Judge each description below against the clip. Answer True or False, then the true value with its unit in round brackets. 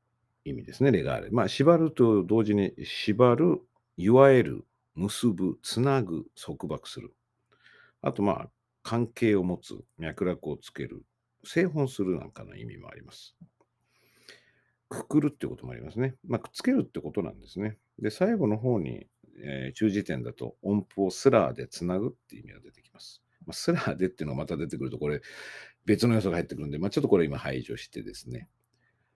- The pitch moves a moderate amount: False (5.7 semitones)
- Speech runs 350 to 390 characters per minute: True (355 characters per minute)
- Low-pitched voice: True (110 Hz)